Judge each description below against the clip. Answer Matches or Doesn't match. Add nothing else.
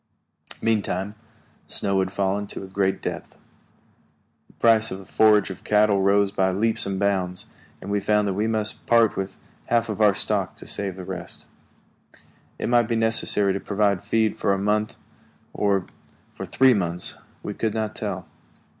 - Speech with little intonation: Matches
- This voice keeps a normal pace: Matches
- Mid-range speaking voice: Doesn't match